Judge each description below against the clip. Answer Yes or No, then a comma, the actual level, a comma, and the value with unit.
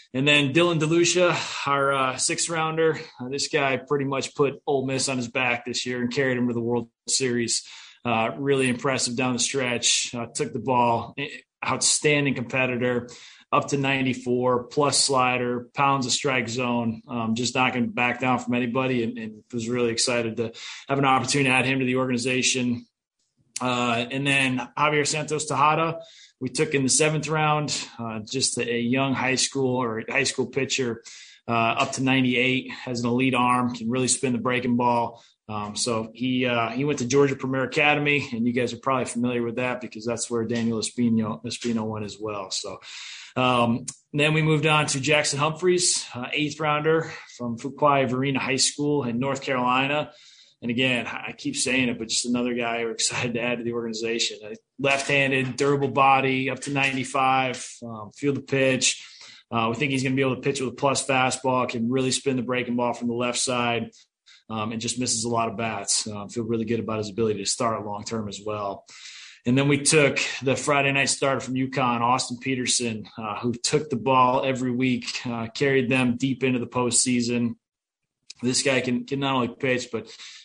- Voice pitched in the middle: No, low, 125 Hz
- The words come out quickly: No, average, 195 wpm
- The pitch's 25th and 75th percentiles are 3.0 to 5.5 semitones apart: No, narrow, 2.4 semitones